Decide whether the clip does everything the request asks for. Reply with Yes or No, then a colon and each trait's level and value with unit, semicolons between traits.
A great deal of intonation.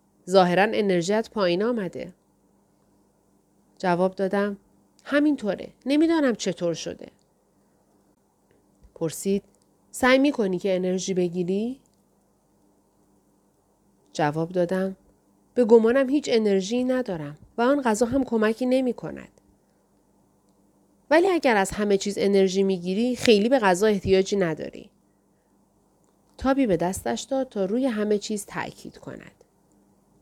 Yes: wide, 7.5 semitones